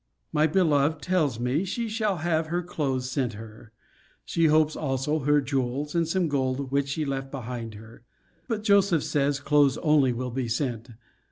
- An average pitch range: Yes, average, 3.7 semitones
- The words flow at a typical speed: Yes, average, 170 wpm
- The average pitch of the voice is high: No, medium, 145 Hz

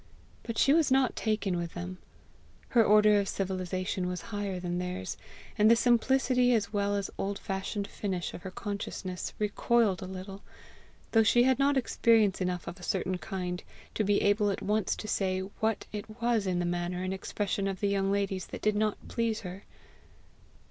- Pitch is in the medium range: No, high, 200 Hz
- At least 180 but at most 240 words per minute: Yes, average, 185 wpm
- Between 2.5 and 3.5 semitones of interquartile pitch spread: Yes, average, 2.8 semitones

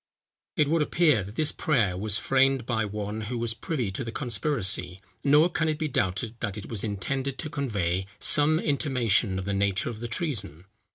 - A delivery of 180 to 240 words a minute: Yes, average, 190 wpm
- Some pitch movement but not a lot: No, wide, 6.0 semitones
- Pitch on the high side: No, low, 115 Hz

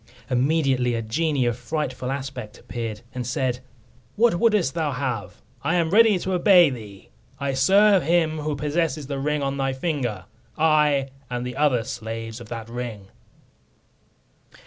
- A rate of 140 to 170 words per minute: Yes, average, 150 wpm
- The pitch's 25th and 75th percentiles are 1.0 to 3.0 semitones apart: No, average, 4.6 semitones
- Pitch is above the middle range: No, low, 135 Hz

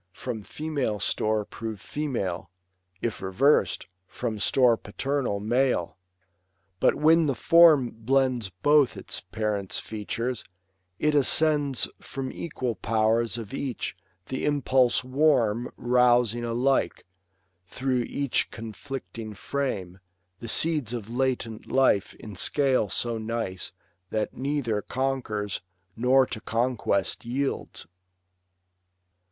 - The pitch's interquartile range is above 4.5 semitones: No, average, 3.8 semitones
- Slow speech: Yes, slow, 105 wpm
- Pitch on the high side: No, low, 120 Hz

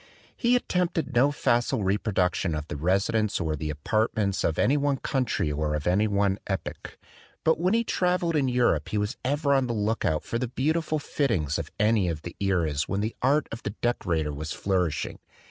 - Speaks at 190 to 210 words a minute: Yes, average, 195 wpm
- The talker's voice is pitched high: No, low, 105 Hz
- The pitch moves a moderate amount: No, wide, 7.9 semitones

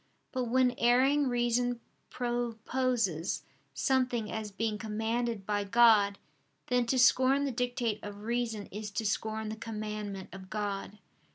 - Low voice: No, high, 225 Hz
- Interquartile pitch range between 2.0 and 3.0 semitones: Yes, narrow, 2.6 semitones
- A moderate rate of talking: No, slow, 130 wpm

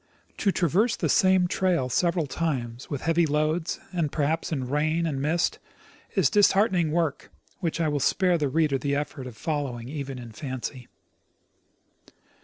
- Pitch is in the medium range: Yes, medium, 155 Hz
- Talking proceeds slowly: No, average, 165 wpm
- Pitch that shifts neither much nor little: Yes, average, 4.0 semitones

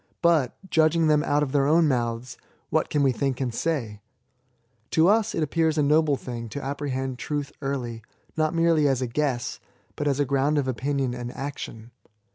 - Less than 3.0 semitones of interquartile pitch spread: No, average, 3.3 semitones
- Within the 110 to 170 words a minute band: No, average, 185 wpm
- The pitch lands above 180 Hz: No, medium, 140 Hz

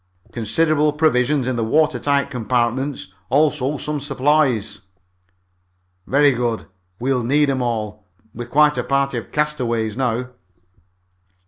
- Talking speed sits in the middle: No, slow, 120 wpm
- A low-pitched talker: Yes, low, 130 Hz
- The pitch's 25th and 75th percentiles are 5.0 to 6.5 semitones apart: No, average, 3.8 semitones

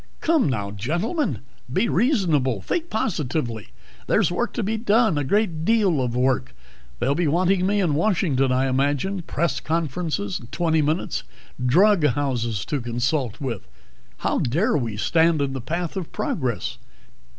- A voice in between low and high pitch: Yes, medium, 155 Hz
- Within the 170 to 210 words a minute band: No, average, 150 wpm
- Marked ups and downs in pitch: Yes, wide, 6.5 semitones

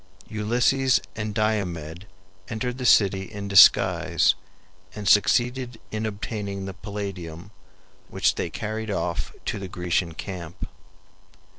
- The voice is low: Yes, low, 100 Hz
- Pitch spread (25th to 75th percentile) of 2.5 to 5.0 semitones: Yes, average, 2.9 semitones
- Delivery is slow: Yes, slow, 115 wpm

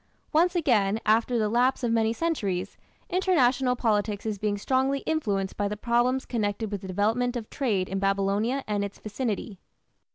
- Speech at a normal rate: Yes, average, 165 wpm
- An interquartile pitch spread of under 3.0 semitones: No, average, 3.9 semitones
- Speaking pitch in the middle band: No, high, 220 Hz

